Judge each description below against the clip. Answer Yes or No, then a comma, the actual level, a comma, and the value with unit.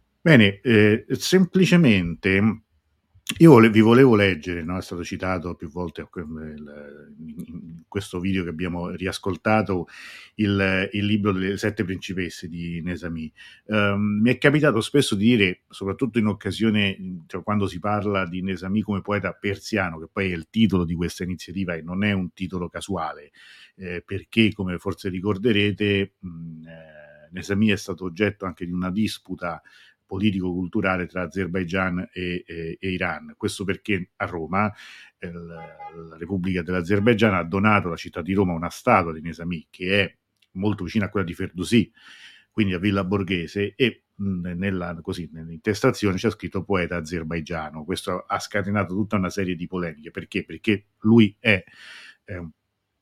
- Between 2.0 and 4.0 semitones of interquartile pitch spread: Yes, average, 2.9 semitones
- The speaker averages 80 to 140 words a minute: No, average, 155 wpm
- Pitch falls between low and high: No, very low, 95 Hz